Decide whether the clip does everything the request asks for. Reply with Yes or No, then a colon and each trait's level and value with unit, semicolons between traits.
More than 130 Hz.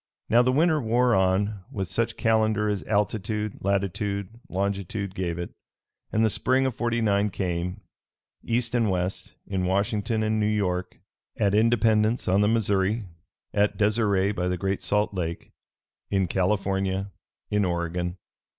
No: low, 100 Hz